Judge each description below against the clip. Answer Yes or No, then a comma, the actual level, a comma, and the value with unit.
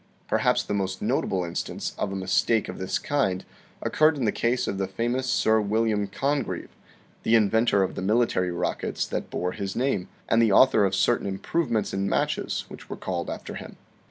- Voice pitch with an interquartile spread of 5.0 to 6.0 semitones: No, average, 3.7 semitones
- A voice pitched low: Yes, low, 105 Hz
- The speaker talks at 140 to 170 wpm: No, average, 185 wpm